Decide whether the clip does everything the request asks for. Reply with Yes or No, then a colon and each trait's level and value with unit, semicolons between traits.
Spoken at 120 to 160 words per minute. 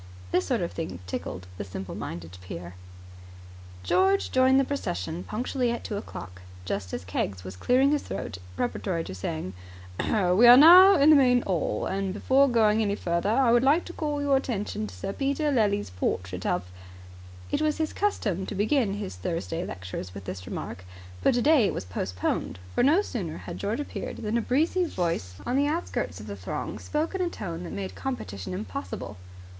No: average, 190 wpm